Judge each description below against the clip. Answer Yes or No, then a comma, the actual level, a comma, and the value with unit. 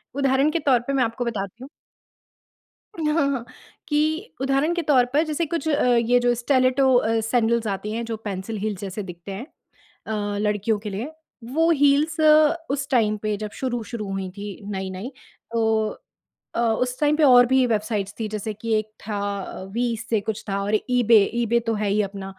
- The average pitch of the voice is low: No, high, 230 Hz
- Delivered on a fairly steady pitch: No, average, 4.1 semitones